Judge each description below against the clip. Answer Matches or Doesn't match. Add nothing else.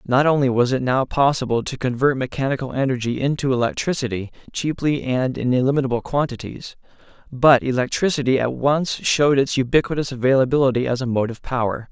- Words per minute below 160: Matches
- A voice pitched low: Matches